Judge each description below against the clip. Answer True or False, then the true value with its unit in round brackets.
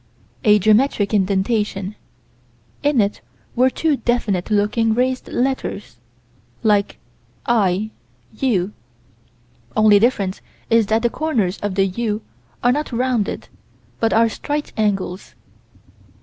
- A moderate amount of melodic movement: True (3.3 semitones)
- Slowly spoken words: True (110 wpm)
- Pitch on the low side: False (215 Hz)